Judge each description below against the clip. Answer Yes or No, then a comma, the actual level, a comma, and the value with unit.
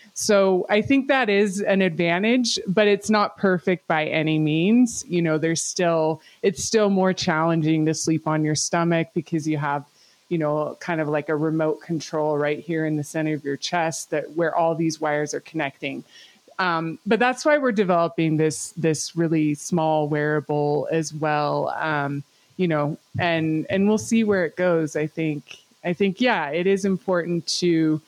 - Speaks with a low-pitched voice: No, medium, 165 Hz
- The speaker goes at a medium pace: Yes, average, 180 wpm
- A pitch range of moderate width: Yes, average, 3.4 semitones